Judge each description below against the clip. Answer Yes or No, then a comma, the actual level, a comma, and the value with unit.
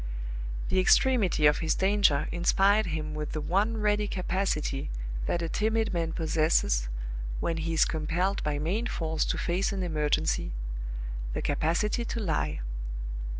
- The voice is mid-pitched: Yes, medium, 170 Hz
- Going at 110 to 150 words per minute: Yes, average, 145 wpm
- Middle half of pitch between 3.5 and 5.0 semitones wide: Yes, average, 4.6 semitones